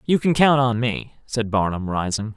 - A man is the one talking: Yes, male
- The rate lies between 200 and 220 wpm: Yes, fast, 205 wpm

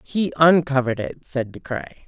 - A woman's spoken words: Yes, female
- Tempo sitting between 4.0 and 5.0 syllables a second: Yes, 4.9 syllables/s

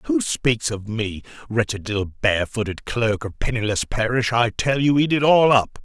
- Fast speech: No, average, 185 wpm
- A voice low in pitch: Yes, low, 115 Hz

